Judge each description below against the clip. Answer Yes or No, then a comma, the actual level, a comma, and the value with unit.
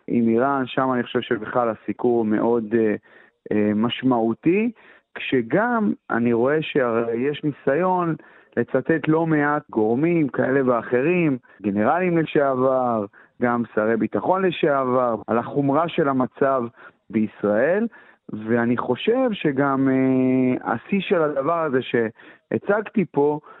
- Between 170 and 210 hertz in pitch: No, low, 130 Hz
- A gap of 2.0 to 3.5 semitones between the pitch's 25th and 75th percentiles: No, average, 5.0 semitones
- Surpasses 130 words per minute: No, average, 110 wpm